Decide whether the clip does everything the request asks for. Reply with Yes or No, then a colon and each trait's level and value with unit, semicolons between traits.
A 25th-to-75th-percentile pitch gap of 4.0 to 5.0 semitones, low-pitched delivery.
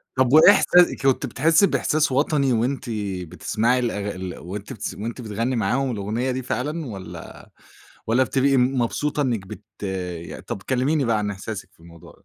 Yes: average, 4.5 semitones; low, 125 Hz